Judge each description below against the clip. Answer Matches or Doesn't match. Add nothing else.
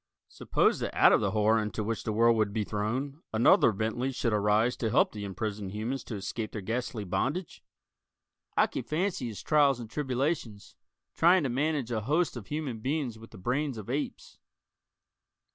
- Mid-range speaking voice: Doesn't match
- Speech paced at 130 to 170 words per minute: Doesn't match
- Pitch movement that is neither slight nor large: Matches